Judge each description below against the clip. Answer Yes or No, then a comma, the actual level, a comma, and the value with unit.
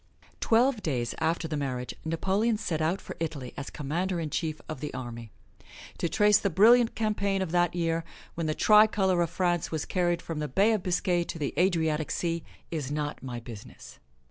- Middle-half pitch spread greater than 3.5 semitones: Yes, average, 4.1 semitones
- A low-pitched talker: No, medium, 165 Hz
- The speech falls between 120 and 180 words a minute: No, average, 190 wpm